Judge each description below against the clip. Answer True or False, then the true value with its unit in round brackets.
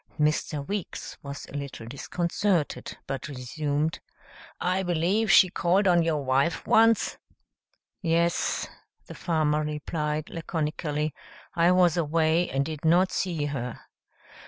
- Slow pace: True (120 wpm)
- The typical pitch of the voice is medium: True (160 Hz)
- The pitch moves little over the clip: False (3.1 semitones)